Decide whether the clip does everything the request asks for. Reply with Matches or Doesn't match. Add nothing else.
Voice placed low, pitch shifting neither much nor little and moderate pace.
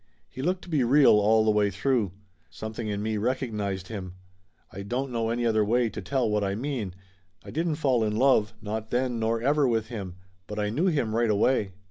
Doesn't match